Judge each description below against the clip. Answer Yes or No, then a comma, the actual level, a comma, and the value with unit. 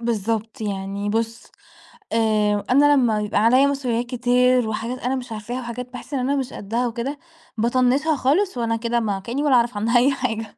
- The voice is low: No, high, 240 Hz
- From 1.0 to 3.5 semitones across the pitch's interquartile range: Yes, narrow, 2.5 semitones